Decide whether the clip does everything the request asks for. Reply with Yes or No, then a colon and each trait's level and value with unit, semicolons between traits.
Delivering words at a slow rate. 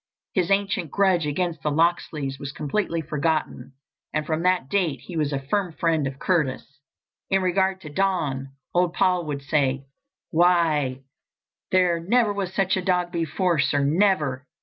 No: average, 155 wpm